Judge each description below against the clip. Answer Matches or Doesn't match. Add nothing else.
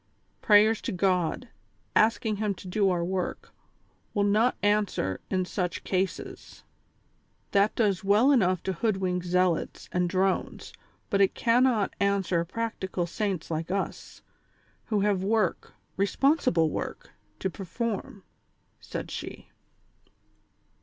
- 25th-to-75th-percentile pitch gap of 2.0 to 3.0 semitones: Matches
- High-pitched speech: Matches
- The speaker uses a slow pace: Matches